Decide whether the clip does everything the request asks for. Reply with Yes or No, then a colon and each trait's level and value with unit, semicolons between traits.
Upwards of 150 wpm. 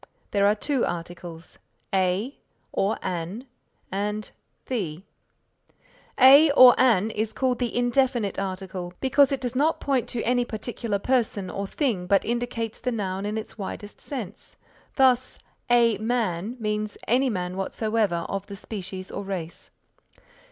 No: average, 140 wpm